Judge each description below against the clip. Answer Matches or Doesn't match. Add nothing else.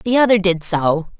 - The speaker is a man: Doesn't match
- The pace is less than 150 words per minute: Doesn't match